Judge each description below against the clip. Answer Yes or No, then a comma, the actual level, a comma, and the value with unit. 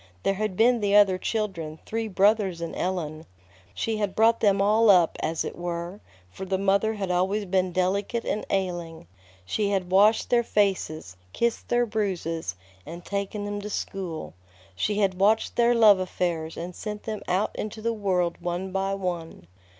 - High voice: Yes, high, 195 Hz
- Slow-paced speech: No, average, 175 wpm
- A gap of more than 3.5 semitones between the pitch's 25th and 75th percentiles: No, average, 3.0 semitones